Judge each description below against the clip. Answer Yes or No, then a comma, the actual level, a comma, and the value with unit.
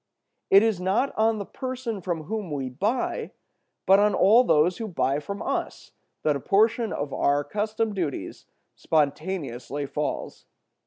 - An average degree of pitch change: No, wide, 6.8 semitones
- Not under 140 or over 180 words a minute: Yes, average, 150 wpm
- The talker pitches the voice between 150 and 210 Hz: Yes, high, 190 Hz